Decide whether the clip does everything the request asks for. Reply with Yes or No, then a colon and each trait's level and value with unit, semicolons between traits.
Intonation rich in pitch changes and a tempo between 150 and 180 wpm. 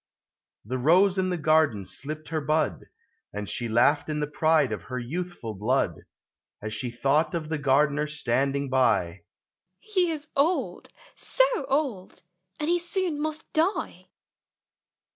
No: wide, 5.9 semitones; slow, 135 wpm